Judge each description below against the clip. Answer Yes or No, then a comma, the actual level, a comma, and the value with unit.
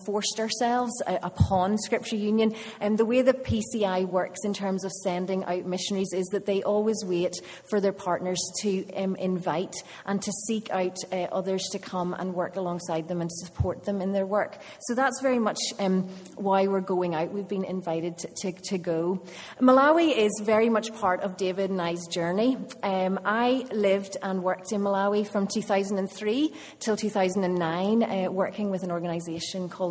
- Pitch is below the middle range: No, high, 195 Hz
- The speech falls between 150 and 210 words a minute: Yes, average, 180 wpm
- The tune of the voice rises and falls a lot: No, narrow, 2.5 semitones